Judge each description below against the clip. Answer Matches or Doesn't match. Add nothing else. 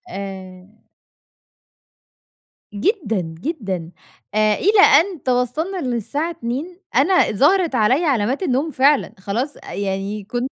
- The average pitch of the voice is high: Matches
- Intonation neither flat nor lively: Doesn't match